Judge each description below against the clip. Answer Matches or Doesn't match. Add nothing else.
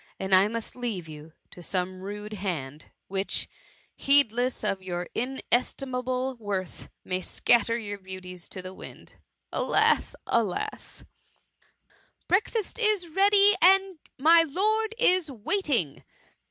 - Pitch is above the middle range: Matches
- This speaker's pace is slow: Matches